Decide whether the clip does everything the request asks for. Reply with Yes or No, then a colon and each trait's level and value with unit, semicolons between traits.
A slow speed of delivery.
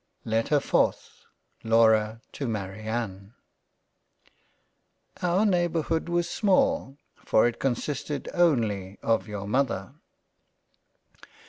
Yes: slow, 85 wpm